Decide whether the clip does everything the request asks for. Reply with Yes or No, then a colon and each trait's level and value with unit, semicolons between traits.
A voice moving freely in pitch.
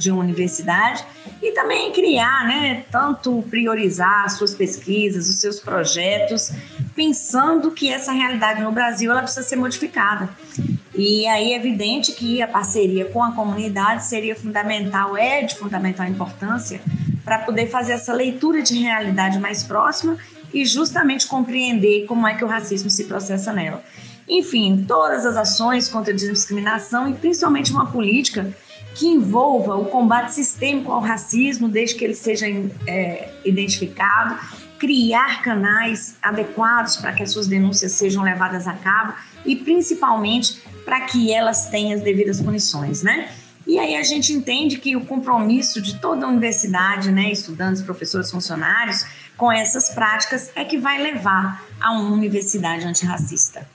No: average, 4.4 semitones